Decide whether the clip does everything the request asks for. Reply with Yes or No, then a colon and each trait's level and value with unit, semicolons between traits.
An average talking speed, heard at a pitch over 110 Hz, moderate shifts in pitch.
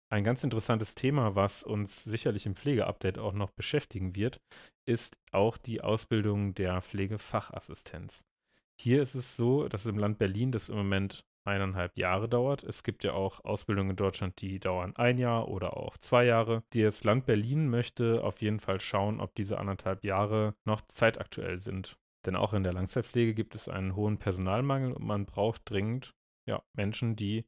No: average, 175 wpm; low, 105 Hz; average, 3.1 semitones